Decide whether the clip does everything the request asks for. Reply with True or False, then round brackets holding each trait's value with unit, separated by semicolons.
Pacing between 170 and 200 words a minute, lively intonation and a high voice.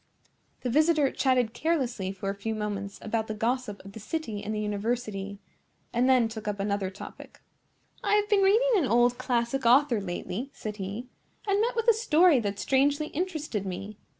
True (180 wpm; 6.1 semitones; 235 Hz)